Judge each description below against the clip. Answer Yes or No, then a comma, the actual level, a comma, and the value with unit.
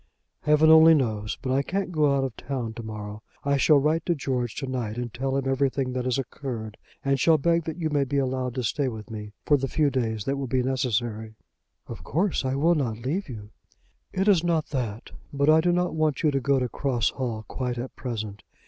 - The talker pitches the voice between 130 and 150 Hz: Yes, low, 135 Hz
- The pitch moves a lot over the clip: No, average, 4.0 semitones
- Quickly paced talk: Yes, fast, 230 wpm